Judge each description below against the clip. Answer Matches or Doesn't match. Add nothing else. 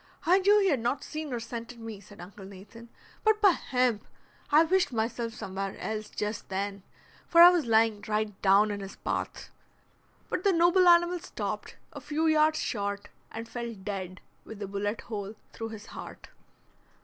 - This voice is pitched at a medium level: Doesn't match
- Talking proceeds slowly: Doesn't match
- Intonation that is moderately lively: Doesn't match